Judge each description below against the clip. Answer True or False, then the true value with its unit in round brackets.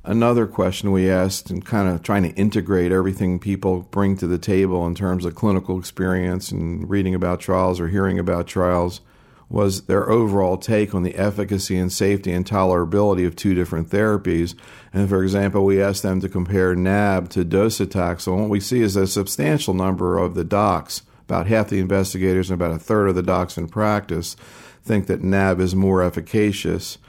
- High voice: False (95 Hz)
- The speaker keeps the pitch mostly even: True (1.9 semitones)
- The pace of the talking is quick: False (185 wpm)